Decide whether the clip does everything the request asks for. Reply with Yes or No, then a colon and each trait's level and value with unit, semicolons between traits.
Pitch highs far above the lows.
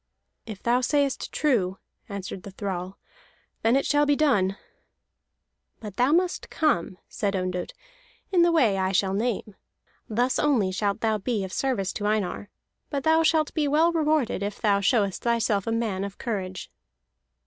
Yes: wide, 6.3 semitones